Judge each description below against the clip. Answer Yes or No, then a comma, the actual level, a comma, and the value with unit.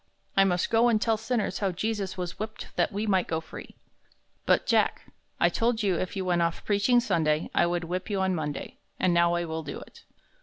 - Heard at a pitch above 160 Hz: Yes, high, 190 Hz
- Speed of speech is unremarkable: No, fast, 225 wpm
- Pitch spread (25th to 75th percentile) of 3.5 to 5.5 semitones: Yes, average, 3.9 semitones